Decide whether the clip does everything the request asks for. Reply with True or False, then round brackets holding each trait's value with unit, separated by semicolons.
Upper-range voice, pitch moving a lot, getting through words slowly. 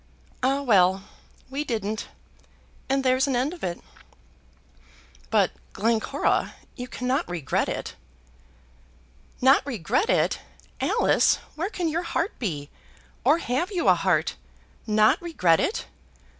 True (250 Hz; 6.7 semitones; 120 wpm)